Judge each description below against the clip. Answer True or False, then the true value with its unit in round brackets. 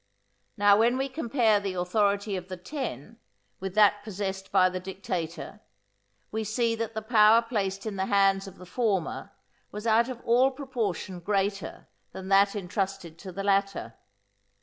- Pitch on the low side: False (200 Hz)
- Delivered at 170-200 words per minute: False (160 wpm)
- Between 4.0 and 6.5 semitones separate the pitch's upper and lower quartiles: False (2.8 semitones)